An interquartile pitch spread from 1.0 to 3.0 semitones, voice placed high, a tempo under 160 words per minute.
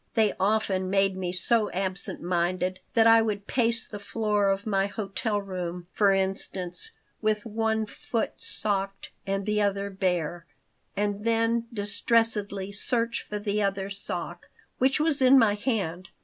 Yes: narrow, 2.5 semitones; high, 205 Hz; average, 150 wpm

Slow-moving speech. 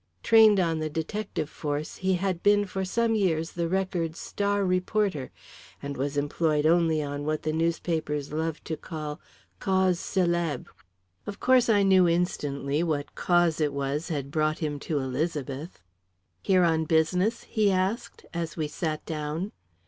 No: average, 155 wpm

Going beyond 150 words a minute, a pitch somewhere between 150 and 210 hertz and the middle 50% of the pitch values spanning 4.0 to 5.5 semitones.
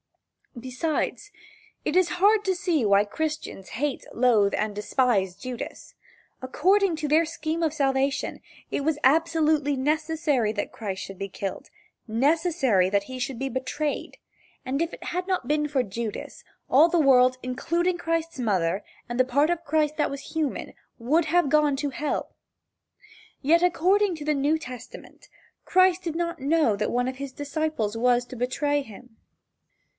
No: average, 160 wpm; very high, 285 Hz; average, 4.6 semitones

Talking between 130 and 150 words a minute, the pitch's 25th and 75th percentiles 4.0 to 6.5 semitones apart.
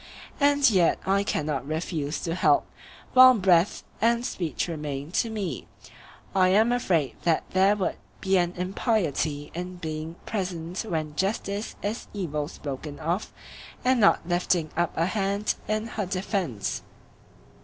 Yes: average, 140 wpm; average, 4.4 semitones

